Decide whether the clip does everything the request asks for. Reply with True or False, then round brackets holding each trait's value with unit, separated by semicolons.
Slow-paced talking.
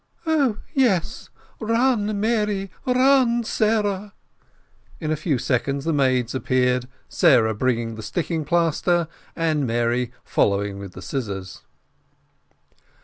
True (110 wpm)